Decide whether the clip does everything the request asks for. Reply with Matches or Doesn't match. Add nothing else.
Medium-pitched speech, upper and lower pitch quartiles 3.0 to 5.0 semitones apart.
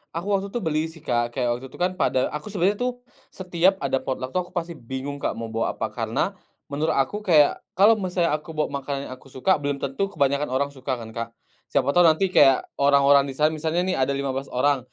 Matches